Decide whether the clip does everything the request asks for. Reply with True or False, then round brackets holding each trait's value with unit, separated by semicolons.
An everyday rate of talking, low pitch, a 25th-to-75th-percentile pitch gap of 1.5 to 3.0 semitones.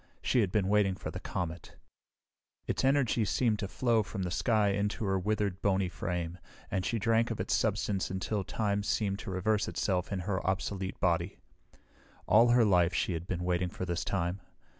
True (185 wpm; 100 Hz; 2.7 semitones)